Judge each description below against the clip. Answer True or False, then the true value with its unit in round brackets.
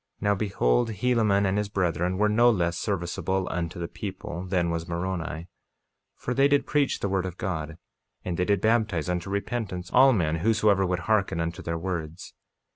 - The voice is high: False (95 Hz)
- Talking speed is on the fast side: False (185 wpm)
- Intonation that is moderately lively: True (3.7 semitones)